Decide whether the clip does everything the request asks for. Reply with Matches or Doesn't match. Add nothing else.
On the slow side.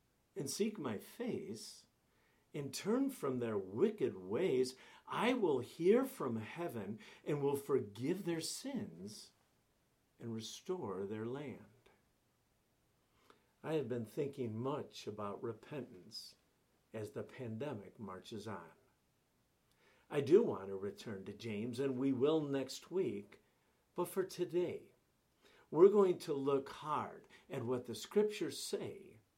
Matches